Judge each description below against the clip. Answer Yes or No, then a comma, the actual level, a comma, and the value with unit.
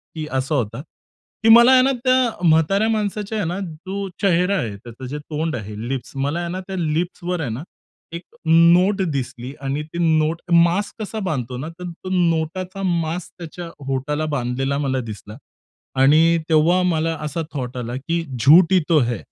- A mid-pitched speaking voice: Yes, medium, 165 Hz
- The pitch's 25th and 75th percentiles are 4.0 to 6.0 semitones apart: Yes, average, 5.1 semitones